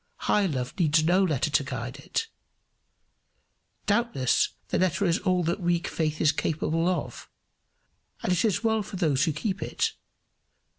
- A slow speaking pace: No, average, 155 wpm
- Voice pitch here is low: No, medium, 170 Hz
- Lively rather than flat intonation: No, average, 4.2 semitones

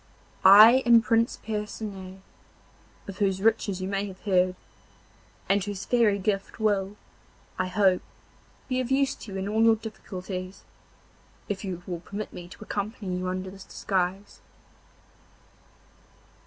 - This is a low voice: No, high, 200 Hz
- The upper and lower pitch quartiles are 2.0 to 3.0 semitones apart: Yes, narrow, 2.4 semitones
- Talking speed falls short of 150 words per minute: Yes, average, 140 wpm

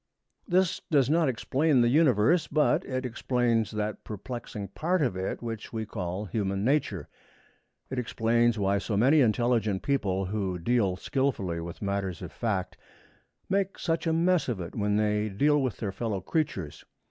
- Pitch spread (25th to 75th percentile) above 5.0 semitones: Yes, wide, 5.6 semitones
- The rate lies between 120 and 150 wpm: No, average, 160 wpm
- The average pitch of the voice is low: Yes, low, 115 Hz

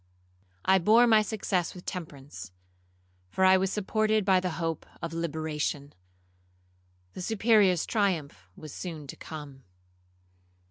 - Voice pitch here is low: No, medium, 180 Hz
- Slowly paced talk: Yes, slow, 125 wpm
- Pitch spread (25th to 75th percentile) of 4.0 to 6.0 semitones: Yes, average, 4.7 semitones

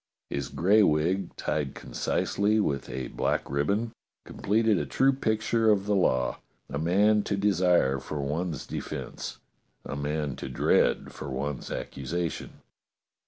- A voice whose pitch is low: Yes, very low, 85 Hz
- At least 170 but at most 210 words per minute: No, average, 140 wpm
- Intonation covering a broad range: Yes, wide, 6.5 semitones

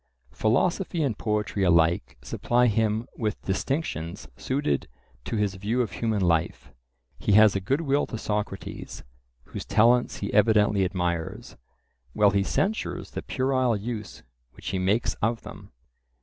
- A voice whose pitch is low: Yes, low, 105 Hz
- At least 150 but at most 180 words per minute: No, average, 140 wpm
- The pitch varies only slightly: No, average, 3.8 semitones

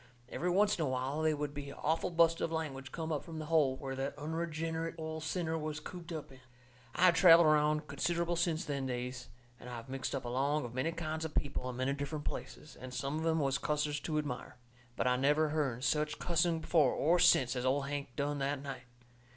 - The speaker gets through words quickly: Yes, fast, 225 wpm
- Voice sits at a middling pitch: Yes, medium, 150 Hz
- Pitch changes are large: No, average, 3.2 semitones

